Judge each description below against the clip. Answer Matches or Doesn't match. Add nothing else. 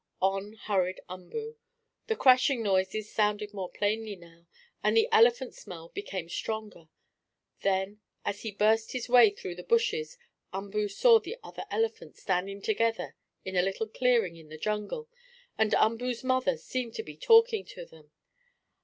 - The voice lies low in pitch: Doesn't match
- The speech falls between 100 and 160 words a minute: Matches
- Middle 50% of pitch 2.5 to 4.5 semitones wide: Doesn't match